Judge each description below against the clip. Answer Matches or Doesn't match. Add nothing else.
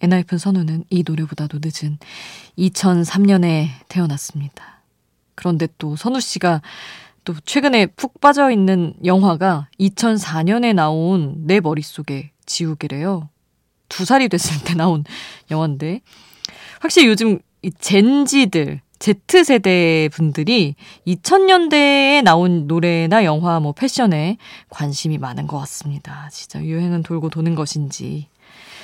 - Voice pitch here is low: Doesn't match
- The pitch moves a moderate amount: Matches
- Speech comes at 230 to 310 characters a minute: Matches